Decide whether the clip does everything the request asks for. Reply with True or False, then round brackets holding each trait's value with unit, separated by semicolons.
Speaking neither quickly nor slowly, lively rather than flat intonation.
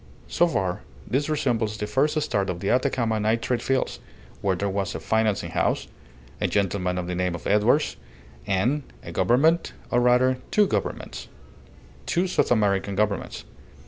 False (155 wpm; 4.9 semitones)